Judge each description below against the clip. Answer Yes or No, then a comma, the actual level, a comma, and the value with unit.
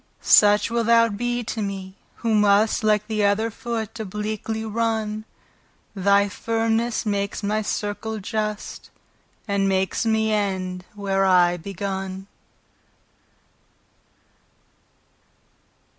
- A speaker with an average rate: No, slow, 100 wpm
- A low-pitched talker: No, high, 210 Hz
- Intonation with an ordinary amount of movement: No, narrow, 1.9 semitones